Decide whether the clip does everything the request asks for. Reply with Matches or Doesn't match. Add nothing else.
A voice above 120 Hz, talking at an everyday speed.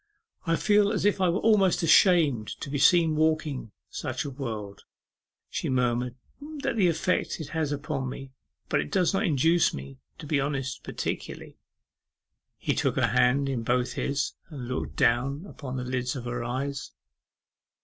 Matches